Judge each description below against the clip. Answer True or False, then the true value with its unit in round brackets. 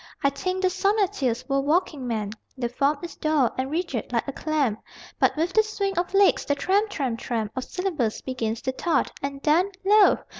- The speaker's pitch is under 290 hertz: False (295 Hz)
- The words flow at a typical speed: True (195 wpm)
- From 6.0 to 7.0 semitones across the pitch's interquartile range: True (6.4 semitones)